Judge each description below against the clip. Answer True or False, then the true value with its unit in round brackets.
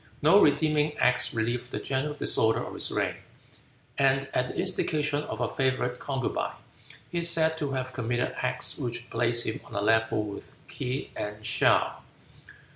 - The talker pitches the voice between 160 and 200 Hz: False (130 Hz)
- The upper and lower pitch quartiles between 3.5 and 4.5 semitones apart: True (3.9 semitones)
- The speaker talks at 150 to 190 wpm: True (165 wpm)